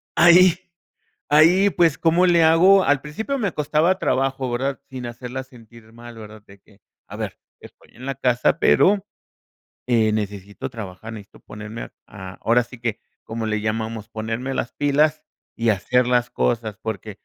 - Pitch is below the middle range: Yes, low, 120 Hz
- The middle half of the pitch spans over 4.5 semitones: Yes, wide, 5.5 semitones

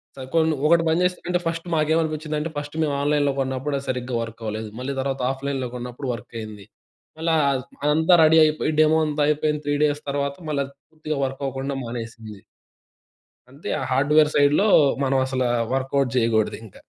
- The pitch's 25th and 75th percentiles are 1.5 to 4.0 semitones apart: Yes, average, 3.1 semitones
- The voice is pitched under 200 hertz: Yes, medium, 140 Hz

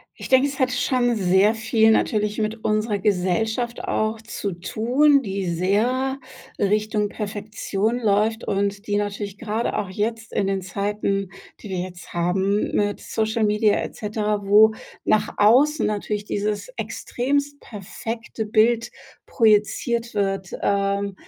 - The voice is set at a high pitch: Yes, high, 210 Hz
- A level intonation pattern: Yes, narrow, 2.2 semitones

